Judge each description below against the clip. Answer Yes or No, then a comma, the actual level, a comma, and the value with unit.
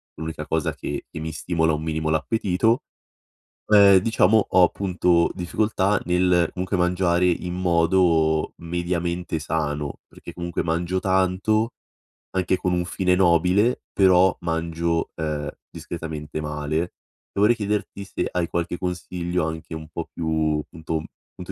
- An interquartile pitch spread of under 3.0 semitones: Yes, narrow, 2.5 semitones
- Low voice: Yes, very low, 85 Hz